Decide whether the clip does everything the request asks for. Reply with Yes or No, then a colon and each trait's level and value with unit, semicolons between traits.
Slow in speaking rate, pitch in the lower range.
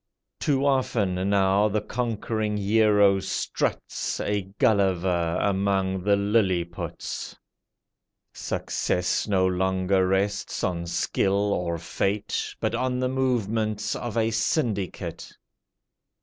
Yes: slow, 100 wpm; low, 100 Hz